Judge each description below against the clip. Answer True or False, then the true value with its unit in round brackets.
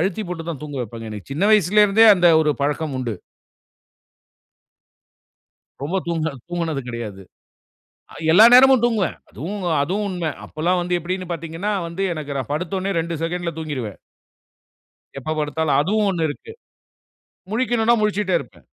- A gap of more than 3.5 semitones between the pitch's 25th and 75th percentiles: True (4.7 semitones)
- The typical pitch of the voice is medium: True (170 Hz)